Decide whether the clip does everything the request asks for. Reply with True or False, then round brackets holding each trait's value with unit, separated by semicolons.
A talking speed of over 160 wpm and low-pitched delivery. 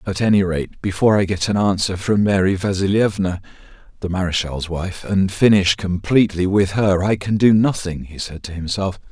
True (180 wpm; 95 Hz)